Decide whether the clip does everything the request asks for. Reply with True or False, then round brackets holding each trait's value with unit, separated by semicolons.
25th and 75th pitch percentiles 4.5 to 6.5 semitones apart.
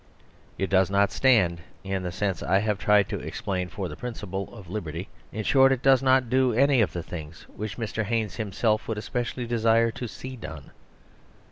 False (4.0 semitones)